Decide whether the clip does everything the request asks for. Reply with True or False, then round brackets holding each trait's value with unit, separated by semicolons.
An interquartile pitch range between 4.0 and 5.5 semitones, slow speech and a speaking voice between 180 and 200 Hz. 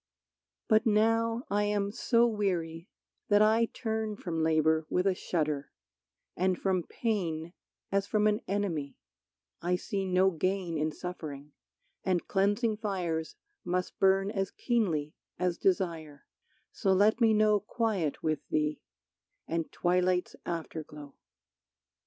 True (4.3 semitones; 125 wpm; 185 Hz)